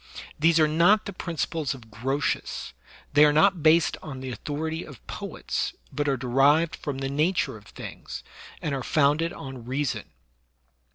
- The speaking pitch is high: No, medium, 145 Hz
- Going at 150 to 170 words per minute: Yes, average, 160 wpm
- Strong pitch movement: No, average, 3.2 semitones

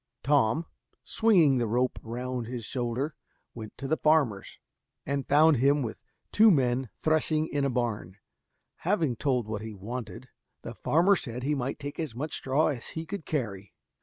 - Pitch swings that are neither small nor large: Yes, average, 4.6 semitones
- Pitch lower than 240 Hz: Yes, low, 135 Hz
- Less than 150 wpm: No, average, 165 wpm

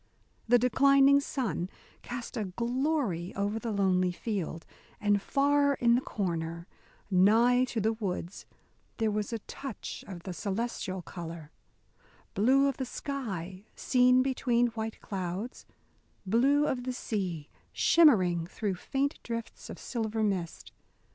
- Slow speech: Yes, slow, 130 wpm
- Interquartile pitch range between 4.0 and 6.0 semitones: Yes, average, 5.2 semitones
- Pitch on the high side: Yes, high, 220 Hz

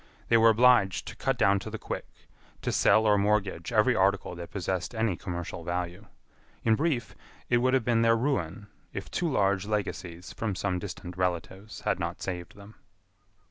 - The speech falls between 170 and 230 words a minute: Yes, average, 180 wpm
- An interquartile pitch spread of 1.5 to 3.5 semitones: No, average, 3.9 semitones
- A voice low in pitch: Yes, low, 100 Hz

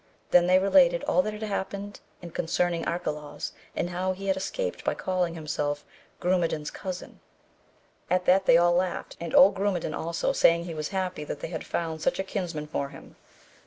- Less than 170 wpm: No, average, 185 wpm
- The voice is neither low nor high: Yes, medium, 180 Hz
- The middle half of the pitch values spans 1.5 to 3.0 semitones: Yes, narrow, 2.6 semitones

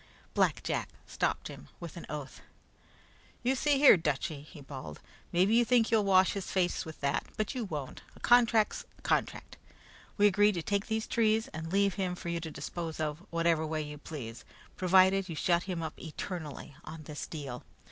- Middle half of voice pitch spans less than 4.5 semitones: No, average, 4.9 semitones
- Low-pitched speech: No, medium, 175 Hz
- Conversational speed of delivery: Yes, average, 190 wpm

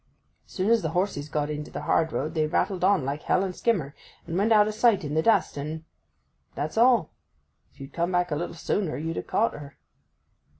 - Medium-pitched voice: Yes, medium, 165 Hz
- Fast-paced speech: Yes, fast, 215 wpm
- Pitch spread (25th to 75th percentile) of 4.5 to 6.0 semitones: Yes, average, 5.0 semitones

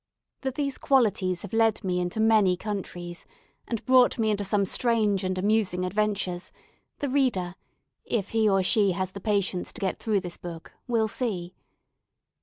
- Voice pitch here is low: No, high, 205 Hz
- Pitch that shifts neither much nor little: Yes, average, 3.3 semitones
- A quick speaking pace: No, average, 165 wpm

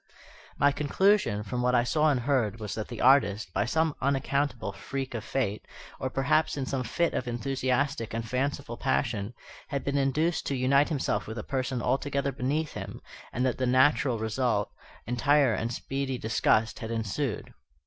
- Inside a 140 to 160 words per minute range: No, average, 170 wpm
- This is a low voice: Yes, low, 130 Hz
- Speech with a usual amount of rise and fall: Yes, average, 3.5 semitones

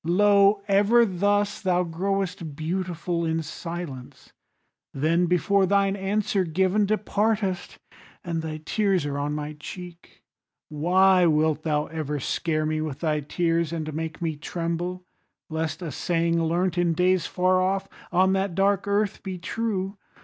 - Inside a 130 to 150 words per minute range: Yes, average, 140 wpm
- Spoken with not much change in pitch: No, average, 3.3 semitones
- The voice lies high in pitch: No, medium, 175 Hz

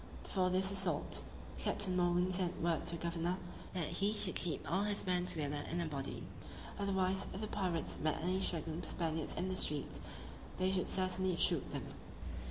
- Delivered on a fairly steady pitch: Yes, narrow, 2.2 semitones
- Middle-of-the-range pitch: Yes, medium, 180 Hz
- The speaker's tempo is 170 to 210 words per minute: Yes, average, 180 wpm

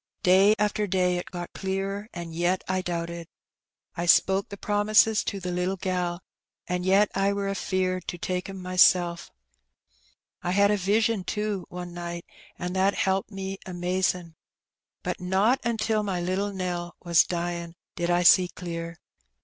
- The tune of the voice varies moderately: No, narrow, 2.0 semitones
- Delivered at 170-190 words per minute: No, average, 155 wpm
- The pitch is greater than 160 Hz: Yes, medium, 185 Hz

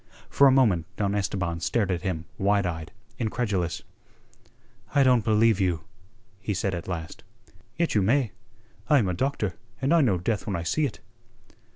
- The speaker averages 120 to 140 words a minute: No, average, 175 wpm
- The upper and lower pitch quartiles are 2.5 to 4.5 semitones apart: No, average, 5.2 semitones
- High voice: No, low, 100 Hz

